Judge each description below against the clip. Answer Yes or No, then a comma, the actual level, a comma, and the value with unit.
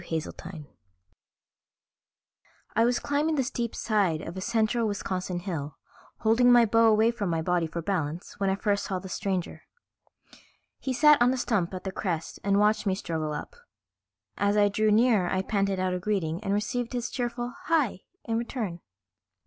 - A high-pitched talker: Yes, high, 205 Hz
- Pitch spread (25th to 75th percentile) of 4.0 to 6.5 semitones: Yes, average, 4.5 semitones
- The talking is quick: No, average, 175 wpm